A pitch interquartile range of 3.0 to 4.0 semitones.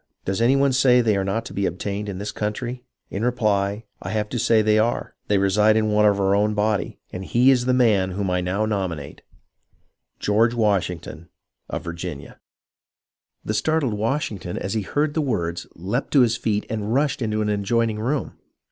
Yes: average, 3.3 semitones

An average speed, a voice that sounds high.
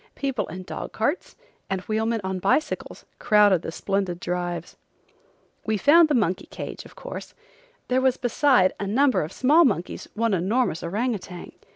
Yes: average, 160 wpm; high, 210 Hz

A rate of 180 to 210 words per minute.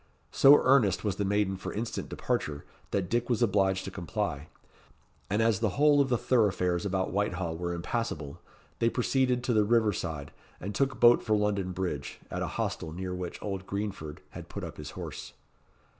Yes: average, 185 wpm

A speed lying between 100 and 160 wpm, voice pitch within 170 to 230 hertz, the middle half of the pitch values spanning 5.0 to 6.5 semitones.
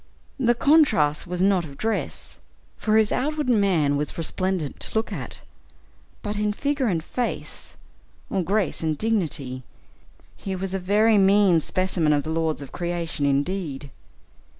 Yes: average, 150 wpm; medium, 185 Hz; average, 5.3 semitones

